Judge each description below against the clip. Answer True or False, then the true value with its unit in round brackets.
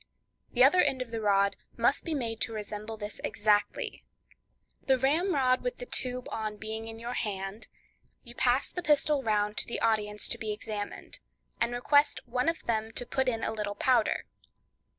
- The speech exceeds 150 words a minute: True (180 wpm)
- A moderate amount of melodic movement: True (3.7 semitones)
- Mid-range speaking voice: False (230 Hz)